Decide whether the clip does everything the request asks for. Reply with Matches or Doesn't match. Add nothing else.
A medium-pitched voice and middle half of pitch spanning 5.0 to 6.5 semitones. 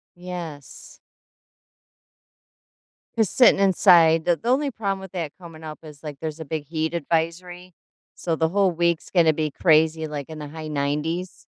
Doesn't match